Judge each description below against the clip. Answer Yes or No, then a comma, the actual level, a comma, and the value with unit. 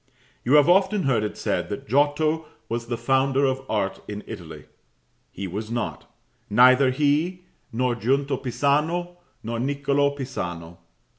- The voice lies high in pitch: No, low, 130 Hz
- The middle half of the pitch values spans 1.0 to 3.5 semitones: No, average, 4.2 semitones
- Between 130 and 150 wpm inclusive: Yes, average, 140 wpm